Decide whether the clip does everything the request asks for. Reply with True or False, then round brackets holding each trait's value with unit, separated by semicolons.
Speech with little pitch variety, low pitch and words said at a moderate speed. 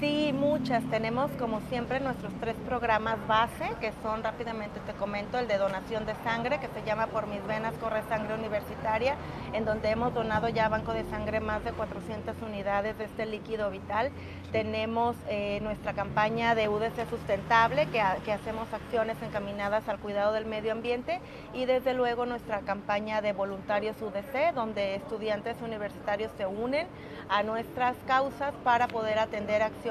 False (1.8 semitones; 220 Hz; 165 wpm)